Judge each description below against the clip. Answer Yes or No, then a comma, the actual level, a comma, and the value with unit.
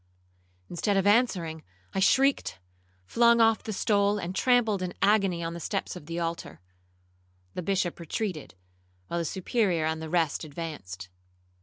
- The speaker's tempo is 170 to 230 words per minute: No, average, 150 wpm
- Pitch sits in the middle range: Yes, medium, 180 Hz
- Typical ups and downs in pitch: Yes, average, 4.0 semitones